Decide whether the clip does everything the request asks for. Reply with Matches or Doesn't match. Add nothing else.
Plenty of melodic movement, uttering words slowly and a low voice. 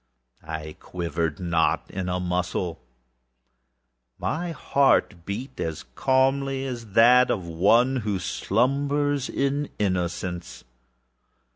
Matches